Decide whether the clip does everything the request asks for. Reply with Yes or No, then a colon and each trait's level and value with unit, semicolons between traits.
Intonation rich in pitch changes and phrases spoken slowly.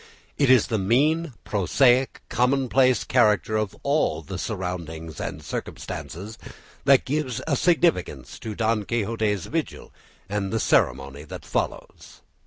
Yes: wide, 5.8 semitones; slow, 125 wpm